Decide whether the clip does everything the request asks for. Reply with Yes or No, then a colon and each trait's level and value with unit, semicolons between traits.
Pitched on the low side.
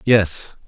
Yes: low, 100 Hz